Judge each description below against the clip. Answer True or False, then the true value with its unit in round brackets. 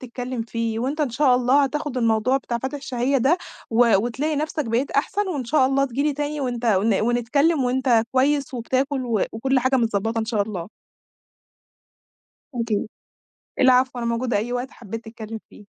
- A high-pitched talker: True (250 Hz)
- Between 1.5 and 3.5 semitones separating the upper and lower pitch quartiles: True (3.1 semitones)